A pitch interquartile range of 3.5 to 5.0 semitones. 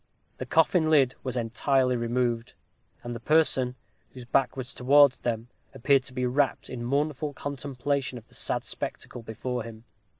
No: average, 2.8 semitones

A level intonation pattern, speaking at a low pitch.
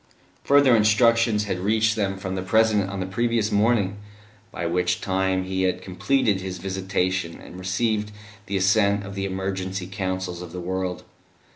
Yes: narrow, 2.3 semitones; very low, 95 Hz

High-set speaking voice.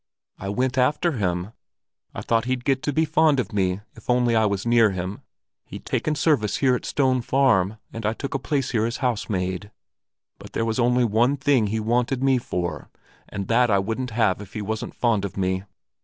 No: low, 115 Hz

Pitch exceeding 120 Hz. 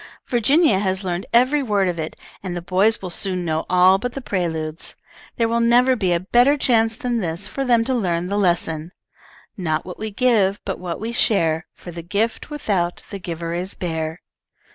Yes: high, 190 Hz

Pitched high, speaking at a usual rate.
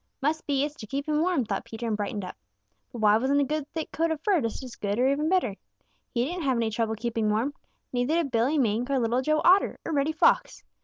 No: very high, 265 Hz; fast, 250 wpm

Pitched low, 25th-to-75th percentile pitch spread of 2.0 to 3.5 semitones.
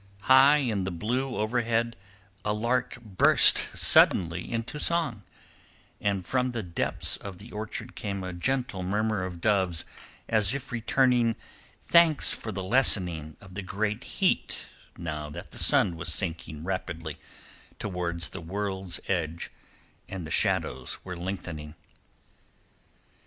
No: low, 100 Hz; average, 5.1 semitones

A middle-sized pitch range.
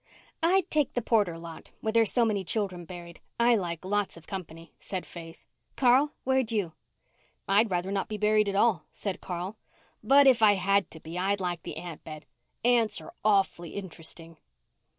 Yes: average, 4.4 semitones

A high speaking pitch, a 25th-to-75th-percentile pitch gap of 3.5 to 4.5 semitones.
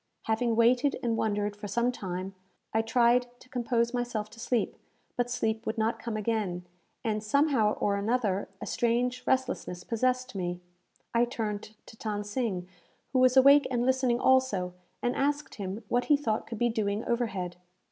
No: high, 230 Hz; average, 3.0 semitones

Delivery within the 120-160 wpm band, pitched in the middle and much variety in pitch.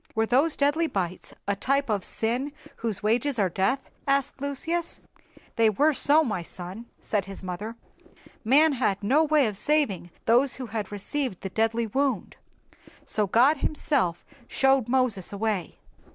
No: average, 155 wpm; high, 235 Hz; wide, 5.7 semitones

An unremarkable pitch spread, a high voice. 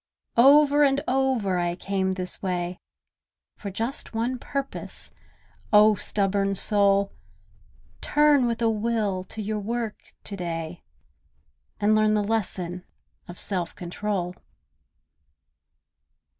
Yes: average, 3.8 semitones; high, 205 Hz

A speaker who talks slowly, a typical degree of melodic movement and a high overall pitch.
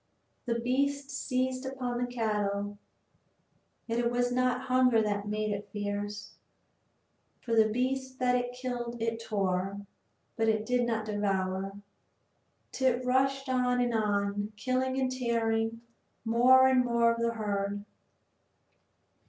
Yes: slow, 130 wpm; average, 3.3 semitones; high, 235 Hz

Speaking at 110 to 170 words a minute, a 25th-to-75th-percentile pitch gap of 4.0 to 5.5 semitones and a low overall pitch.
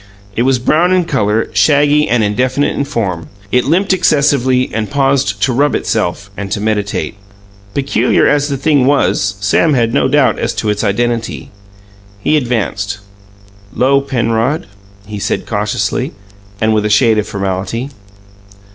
Yes: average, 150 wpm; average, 5.2 semitones; low, 120 Hz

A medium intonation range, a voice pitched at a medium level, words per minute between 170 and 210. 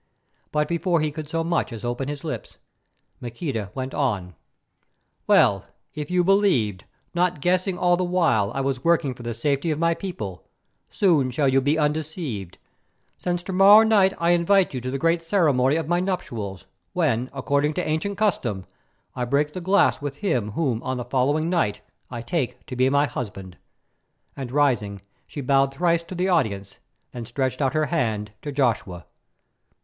No: wide, 5.7 semitones; medium, 145 Hz; average, 175 wpm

